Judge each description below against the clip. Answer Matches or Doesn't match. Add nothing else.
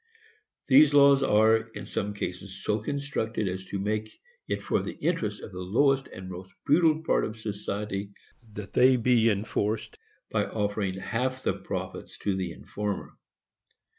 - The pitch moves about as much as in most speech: Matches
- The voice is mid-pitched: Doesn't match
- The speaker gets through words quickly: Doesn't match